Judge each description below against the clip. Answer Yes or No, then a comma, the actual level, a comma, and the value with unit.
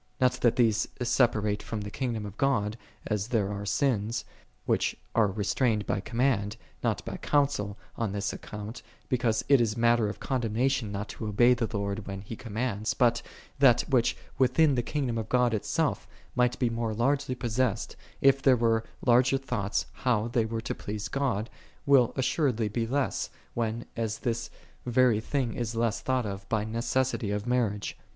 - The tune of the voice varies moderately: Yes, average, 3.1 semitones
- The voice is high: No, low, 115 Hz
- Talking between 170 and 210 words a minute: Yes, average, 175 wpm